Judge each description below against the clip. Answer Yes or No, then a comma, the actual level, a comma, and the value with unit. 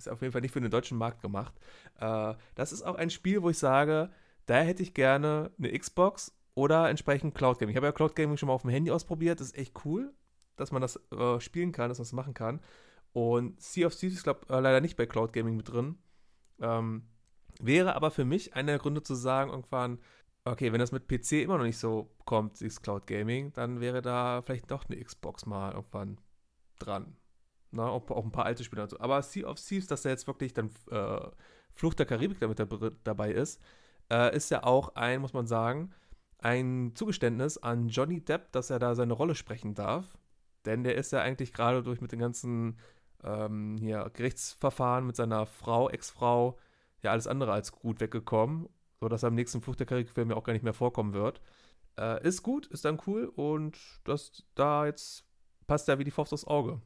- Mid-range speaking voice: No, low, 125 Hz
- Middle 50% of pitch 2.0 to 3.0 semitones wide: No, average, 4.3 semitones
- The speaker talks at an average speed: No, fast, 210 wpm